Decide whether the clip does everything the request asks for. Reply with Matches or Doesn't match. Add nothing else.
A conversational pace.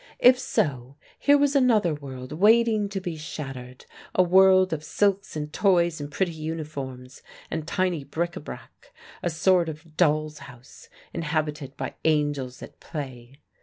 Matches